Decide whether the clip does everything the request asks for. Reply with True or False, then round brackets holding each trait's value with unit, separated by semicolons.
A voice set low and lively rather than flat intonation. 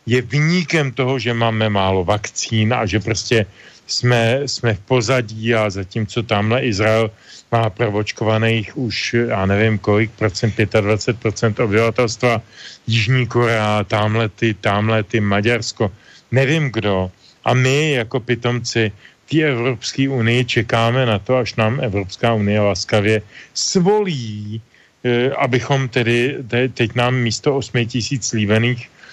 False (115 Hz; 2.6 semitones)